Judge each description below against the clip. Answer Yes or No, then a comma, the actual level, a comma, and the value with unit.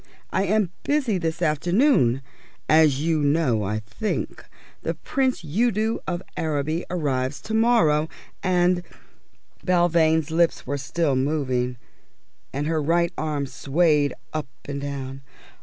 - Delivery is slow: Yes, slow, 125 wpm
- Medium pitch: Yes, medium, 160 Hz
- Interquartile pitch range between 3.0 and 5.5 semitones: Yes, average, 3.9 semitones